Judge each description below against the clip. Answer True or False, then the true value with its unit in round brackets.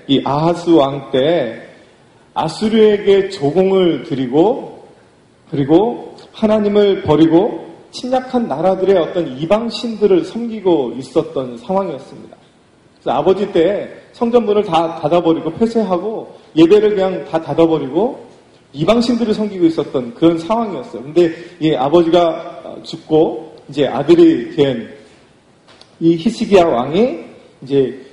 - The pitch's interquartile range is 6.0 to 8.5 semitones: False (5.2 semitones)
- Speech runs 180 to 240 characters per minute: False (275 characters per minute)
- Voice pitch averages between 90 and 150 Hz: False (175 Hz)